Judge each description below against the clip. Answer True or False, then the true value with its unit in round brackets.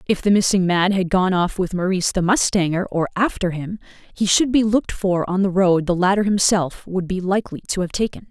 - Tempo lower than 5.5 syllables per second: False (5.6 syllables/s)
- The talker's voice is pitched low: False (190 Hz)